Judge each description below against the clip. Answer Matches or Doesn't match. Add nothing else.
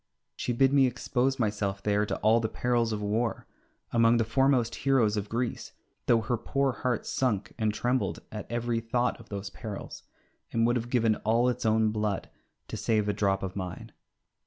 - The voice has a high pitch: Doesn't match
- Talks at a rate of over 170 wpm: Matches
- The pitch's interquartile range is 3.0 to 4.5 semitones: Doesn't match